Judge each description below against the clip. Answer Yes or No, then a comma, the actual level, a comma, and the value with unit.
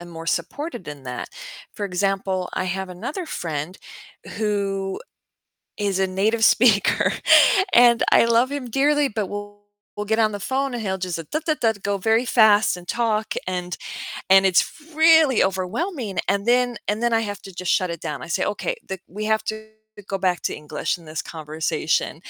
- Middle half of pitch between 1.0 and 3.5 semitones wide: No, average, 4.0 semitones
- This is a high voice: Yes, high, 205 Hz